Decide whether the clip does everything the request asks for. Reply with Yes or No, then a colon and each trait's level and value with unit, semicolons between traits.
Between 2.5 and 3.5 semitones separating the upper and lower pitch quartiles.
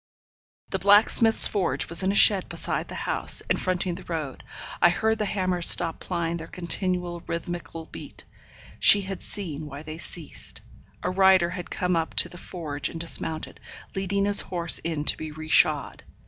Yes: average, 2.8 semitones